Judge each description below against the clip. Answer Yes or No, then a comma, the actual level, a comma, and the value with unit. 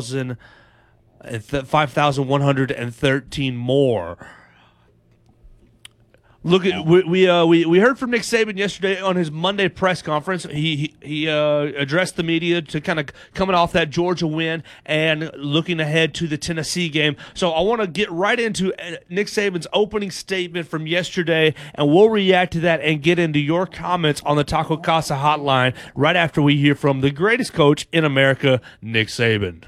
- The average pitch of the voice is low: No, medium, 160 Hz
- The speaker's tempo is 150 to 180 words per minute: Yes, average, 165 wpm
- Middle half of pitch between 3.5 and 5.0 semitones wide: Yes, average, 4.1 semitones